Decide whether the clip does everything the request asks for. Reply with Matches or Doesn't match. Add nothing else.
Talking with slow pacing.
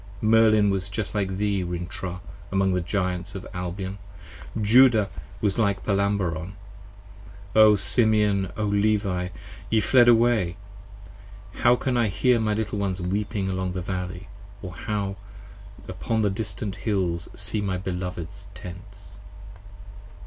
Matches